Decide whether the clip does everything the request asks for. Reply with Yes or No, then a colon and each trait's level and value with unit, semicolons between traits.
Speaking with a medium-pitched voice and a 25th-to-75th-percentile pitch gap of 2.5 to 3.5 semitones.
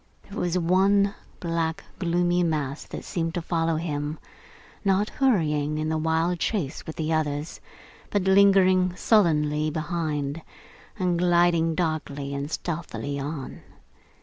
Yes: medium, 165 Hz; average, 2.8 semitones